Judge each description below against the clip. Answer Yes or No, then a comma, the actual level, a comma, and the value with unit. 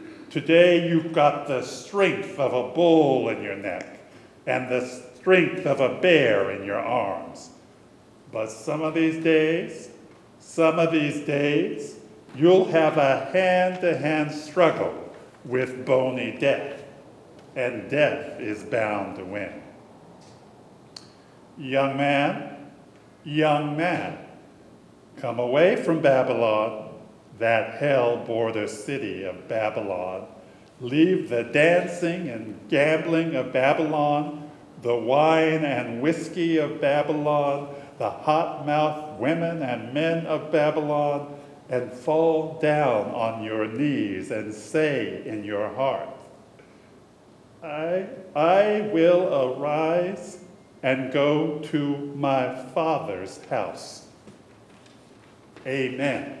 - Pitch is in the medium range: Yes, medium, 150 Hz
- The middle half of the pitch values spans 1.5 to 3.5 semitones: No, average, 4.0 semitones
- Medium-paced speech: No, slow, 110 wpm